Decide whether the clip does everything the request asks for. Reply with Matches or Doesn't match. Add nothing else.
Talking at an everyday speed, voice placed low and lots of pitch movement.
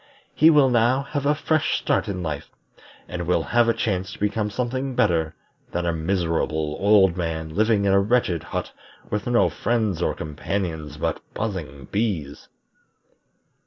Matches